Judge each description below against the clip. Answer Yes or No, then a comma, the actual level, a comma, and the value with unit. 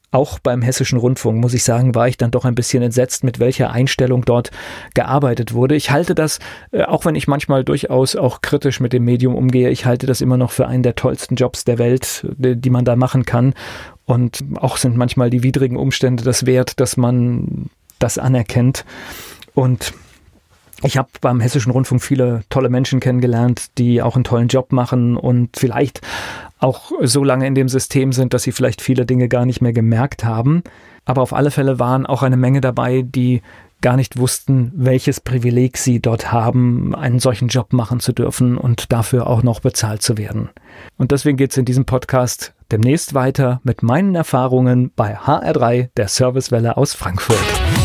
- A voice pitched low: Yes, low, 125 Hz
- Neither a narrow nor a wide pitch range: No, narrow, 1.3 semitones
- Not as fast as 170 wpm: No, average, 185 wpm